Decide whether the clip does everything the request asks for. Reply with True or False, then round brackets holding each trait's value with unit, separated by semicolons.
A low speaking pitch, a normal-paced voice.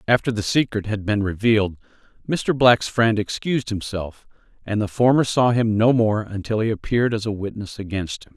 True (110 Hz; 185 wpm)